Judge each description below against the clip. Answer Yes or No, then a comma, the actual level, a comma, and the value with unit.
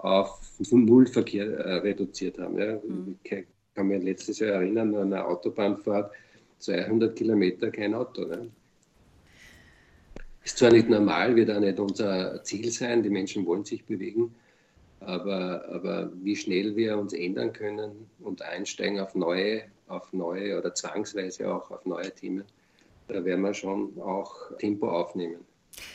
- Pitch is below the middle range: Yes, low, 100 Hz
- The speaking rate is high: No, average, 145 wpm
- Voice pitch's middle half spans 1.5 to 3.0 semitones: Yes, narrow, 2.4 semitones